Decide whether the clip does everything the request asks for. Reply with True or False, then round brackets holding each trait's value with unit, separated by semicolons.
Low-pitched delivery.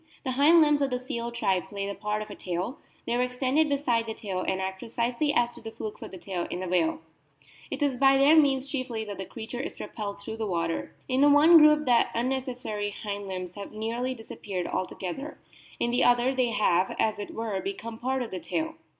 False (235 Hz)